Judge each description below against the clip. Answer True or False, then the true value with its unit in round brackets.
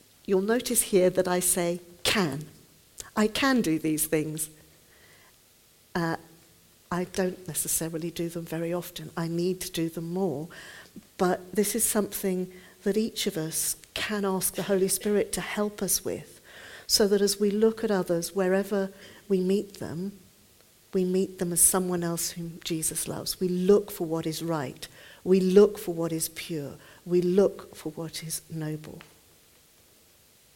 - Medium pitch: True (180 Hz)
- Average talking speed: True (160 wpm)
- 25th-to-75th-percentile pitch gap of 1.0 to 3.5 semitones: True (3.1 semitones)